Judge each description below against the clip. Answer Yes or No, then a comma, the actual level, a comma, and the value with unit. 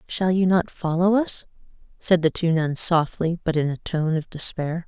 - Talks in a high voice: No, medium, 170 Hz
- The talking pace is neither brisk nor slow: Yes, average, 195 wpm